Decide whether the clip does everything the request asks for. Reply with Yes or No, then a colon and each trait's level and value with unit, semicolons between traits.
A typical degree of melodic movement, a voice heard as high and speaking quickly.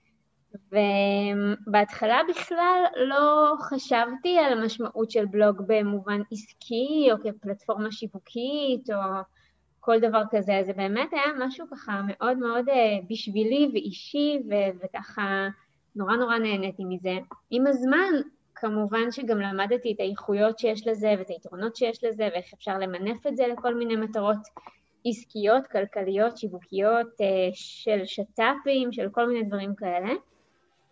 No: average, 3.5 semitones; high, 220 Hz; average, 120 wpm